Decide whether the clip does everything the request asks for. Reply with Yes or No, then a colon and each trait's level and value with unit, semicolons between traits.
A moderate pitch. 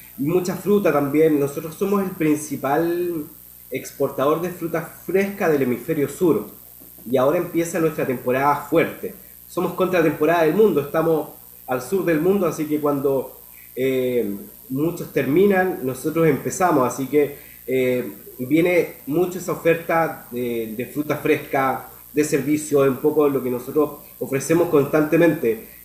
Yes: medium, 150 Hz